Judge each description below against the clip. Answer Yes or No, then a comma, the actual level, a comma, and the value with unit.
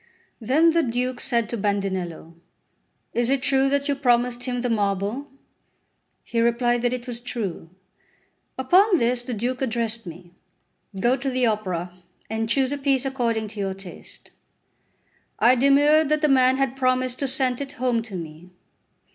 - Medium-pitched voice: No, high, 245 Hz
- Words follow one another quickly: No, average, 165 wpm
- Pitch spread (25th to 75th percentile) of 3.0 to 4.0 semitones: Yes, average, 3.3 semitones